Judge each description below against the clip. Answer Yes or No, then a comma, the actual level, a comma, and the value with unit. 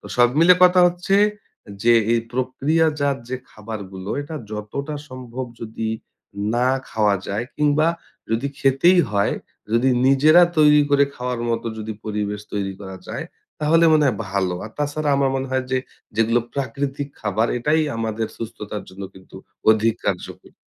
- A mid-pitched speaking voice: No, low, 125 Hz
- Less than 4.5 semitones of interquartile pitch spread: No, average, 5.2 semitones